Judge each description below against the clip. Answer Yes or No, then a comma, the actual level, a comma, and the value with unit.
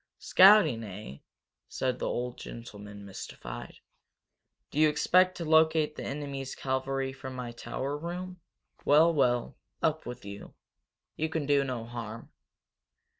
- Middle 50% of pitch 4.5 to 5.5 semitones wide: Yes, average, 4.9 semitones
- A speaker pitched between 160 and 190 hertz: No, low, 135 Hz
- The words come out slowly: Yes, slow, 130 wpm